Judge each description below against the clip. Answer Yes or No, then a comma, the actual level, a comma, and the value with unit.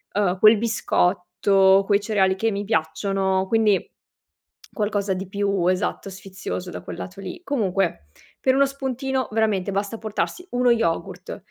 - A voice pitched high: Yes, high, 200 Hz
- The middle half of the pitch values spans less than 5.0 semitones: Yes, average, 2.7 semitones